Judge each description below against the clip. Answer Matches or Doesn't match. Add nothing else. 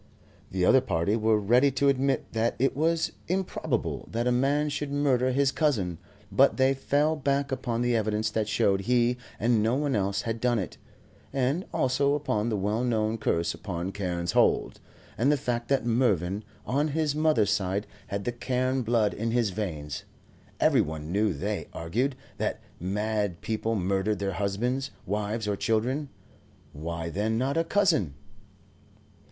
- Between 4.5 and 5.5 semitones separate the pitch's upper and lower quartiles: Matches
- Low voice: Matches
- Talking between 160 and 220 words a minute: Matches